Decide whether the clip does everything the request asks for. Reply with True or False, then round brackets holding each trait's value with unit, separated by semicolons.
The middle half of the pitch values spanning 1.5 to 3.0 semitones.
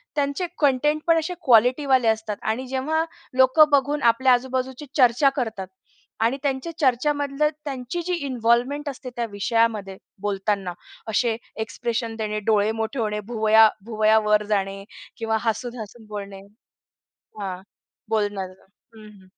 False (3.9 semitones)